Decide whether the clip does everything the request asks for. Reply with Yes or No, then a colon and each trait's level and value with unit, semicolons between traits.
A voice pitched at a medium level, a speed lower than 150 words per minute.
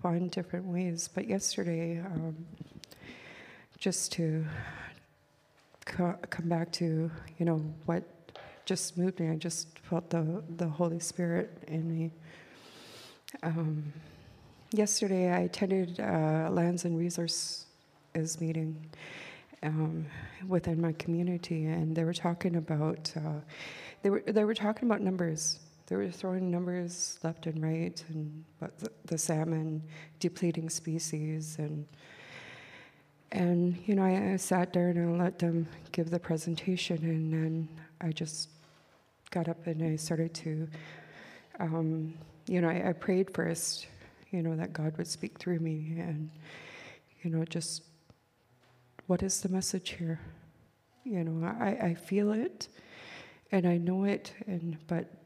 Yes: medium, 165 Hz; average, 140 wpm